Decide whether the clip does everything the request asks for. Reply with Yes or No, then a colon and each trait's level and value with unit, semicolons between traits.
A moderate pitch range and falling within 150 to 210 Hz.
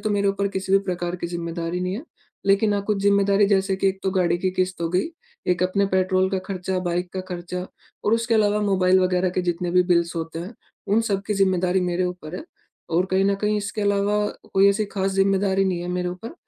No: narrow, 1.9 semitones; high, 190 Hz